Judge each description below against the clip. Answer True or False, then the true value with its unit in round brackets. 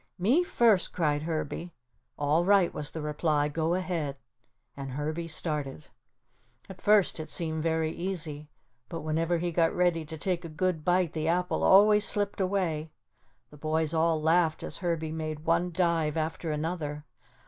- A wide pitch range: False (2.4 semitones)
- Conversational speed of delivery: True (160 wpm)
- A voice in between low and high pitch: True (165 Hz)